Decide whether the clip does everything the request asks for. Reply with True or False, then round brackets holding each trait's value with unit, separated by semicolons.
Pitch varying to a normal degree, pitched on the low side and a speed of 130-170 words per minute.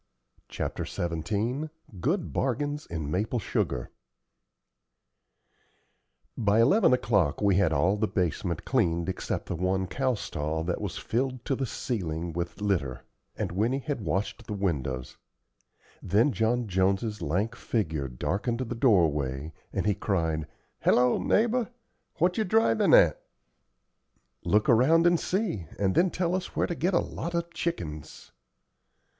False (7.6 semitones; 105 Hz; 140 wpm)